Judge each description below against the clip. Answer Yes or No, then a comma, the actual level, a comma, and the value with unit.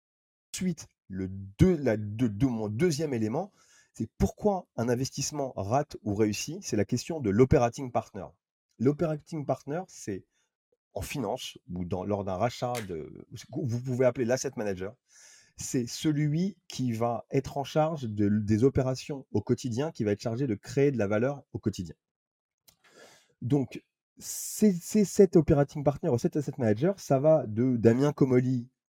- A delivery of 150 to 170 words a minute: Yes, average, 160 wpm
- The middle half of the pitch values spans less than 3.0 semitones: No, average, 5.0 semitones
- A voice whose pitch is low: Yes, low, 130 Hz